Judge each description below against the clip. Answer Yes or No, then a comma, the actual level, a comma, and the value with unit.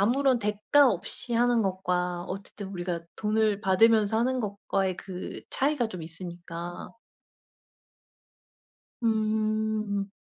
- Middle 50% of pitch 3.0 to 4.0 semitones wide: Yes, average, 3.3 semitones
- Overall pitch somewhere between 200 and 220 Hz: Yes, high, 205 Hz